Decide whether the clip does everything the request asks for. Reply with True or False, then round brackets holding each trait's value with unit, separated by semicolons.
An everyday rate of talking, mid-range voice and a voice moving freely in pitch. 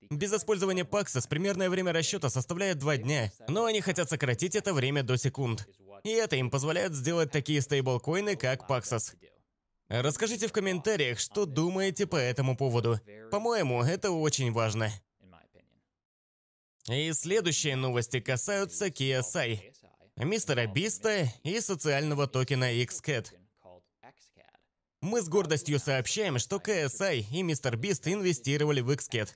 True (125 wpm; 145 Hz; 7.0 semitones)